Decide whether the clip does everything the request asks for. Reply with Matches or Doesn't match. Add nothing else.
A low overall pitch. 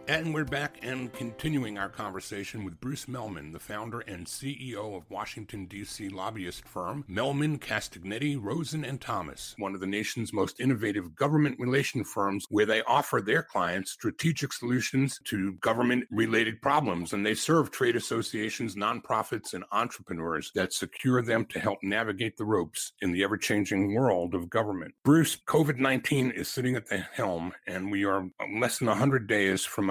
Matches